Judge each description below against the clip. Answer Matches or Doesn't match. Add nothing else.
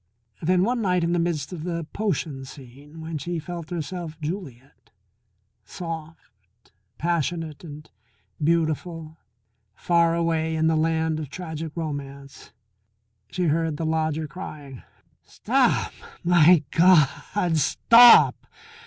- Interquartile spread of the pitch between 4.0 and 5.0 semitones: Doesn't match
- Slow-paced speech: Matches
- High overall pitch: Doesn't match